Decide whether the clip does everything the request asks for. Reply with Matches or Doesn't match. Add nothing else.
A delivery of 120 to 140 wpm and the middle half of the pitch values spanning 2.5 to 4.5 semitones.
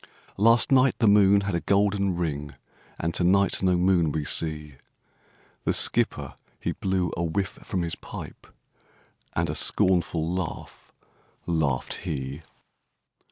Matches